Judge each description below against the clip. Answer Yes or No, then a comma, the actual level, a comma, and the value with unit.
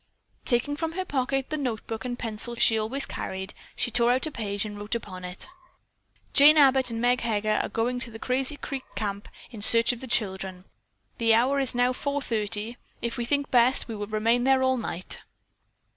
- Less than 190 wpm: No, average, 195 wpm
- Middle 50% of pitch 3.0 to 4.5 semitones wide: Yes, average, 3.4 semitones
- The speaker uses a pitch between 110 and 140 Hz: No, high, 235 Hz